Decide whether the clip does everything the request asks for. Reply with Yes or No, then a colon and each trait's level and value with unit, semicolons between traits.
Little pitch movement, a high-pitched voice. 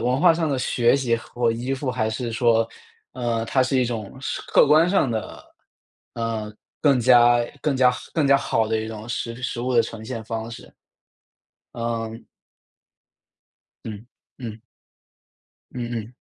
No: narrow, 2.3 semitones; low, 120 Hz